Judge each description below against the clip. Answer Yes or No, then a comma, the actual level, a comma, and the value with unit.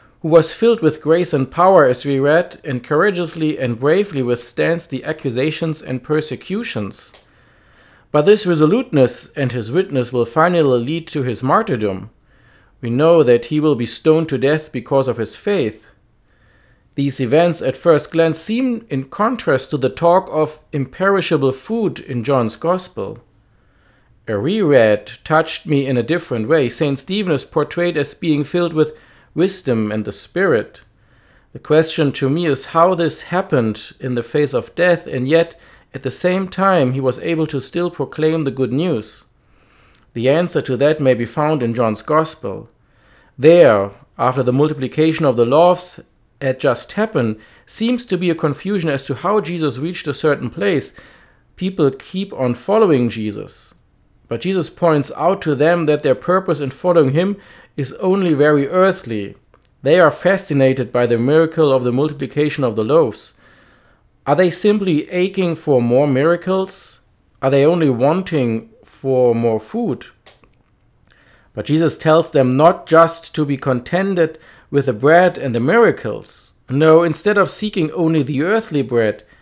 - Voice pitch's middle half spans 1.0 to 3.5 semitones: No, average, 4.8 semitones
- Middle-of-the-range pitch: Yes, medium, 150 Hz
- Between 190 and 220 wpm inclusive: No, average, 160 wpm